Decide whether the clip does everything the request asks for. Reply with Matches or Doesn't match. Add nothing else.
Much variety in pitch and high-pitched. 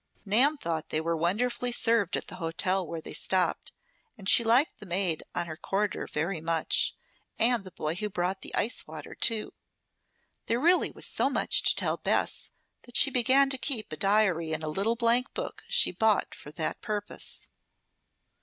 Matches